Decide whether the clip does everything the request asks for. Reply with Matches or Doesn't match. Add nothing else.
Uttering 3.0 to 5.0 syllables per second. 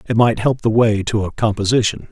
Doesn't match